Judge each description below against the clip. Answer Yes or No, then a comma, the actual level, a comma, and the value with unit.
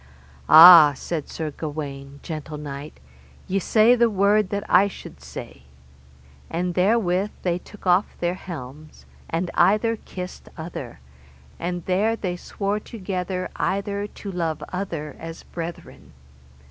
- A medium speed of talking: No, slow, 130 wpm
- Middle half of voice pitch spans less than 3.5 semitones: No, average, 4.0 semitones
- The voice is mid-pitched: Yes, medium, 180 Hz